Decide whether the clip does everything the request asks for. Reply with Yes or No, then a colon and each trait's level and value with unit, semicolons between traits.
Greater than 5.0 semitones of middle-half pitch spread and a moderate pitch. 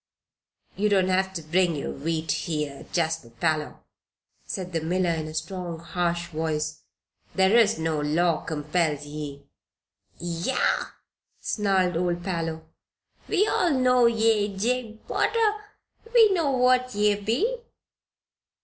Yes: wide, 5.4 semitones; medium, 180 Hz